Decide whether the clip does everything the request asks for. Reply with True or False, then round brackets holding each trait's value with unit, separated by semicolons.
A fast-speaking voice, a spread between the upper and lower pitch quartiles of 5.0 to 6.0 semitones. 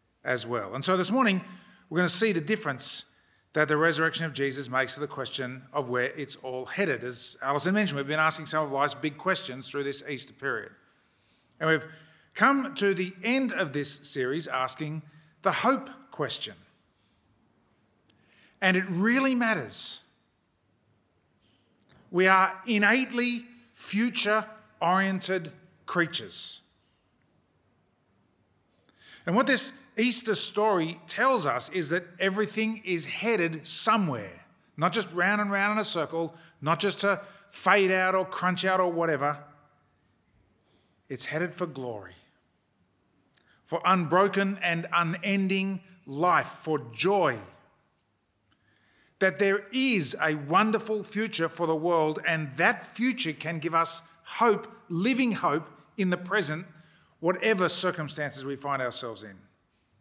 False (135 wpm; 5.4 semitones)